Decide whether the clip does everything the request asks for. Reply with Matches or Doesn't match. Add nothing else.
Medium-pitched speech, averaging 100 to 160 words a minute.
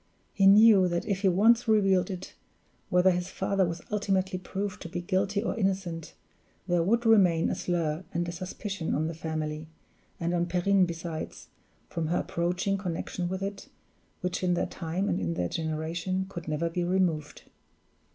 Doesn't match